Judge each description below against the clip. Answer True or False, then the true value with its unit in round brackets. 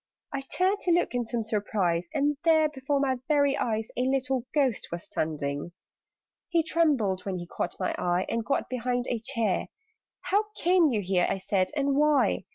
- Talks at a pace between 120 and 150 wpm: False (180 wpm)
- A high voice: True (250 Hz)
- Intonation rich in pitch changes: True (6.7 semitones)